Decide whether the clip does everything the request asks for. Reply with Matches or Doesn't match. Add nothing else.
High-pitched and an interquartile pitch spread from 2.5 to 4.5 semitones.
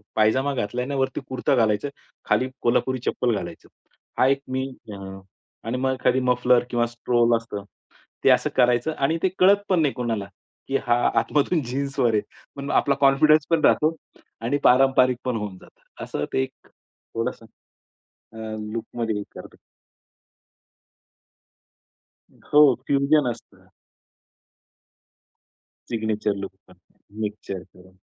Doesn't match